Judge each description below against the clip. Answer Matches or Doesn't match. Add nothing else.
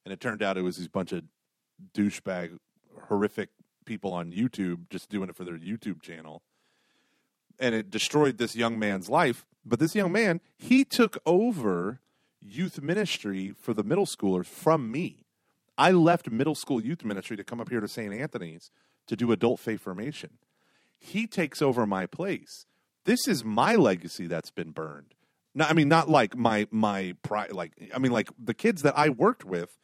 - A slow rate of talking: Doesn't match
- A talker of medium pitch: Doesn't match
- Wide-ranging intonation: Matches